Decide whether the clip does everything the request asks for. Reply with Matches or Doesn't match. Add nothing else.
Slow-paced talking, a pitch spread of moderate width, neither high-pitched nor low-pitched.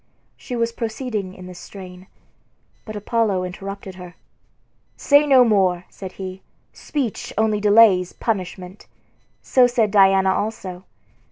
Doesn't match